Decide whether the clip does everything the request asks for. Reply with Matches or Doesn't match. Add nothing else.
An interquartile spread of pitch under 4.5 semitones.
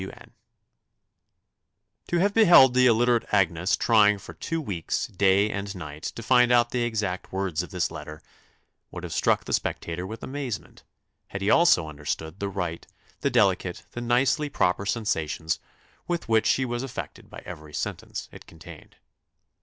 Doesn't match